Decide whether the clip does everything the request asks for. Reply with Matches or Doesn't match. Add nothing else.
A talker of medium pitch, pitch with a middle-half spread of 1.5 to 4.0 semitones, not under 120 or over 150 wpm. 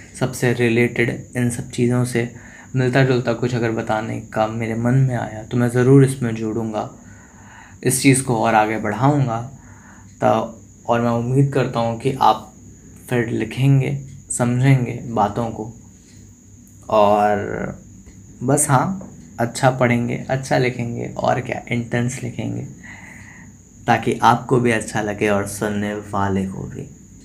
Doesn't match